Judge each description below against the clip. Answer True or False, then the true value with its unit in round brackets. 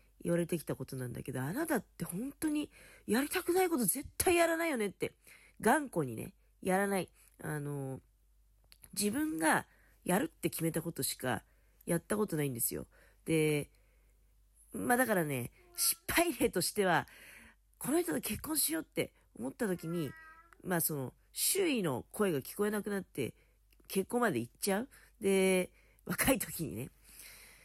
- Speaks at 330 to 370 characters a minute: False (295 characters per minute)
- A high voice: True (195 Hz)